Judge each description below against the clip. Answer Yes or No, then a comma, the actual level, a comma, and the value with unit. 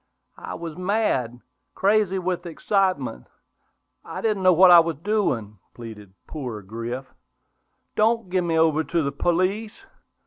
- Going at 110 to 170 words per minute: Yes, slow, 135 wpm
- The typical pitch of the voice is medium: Yes, medium, 170 Hz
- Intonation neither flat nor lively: No, wide, 7.1 semitones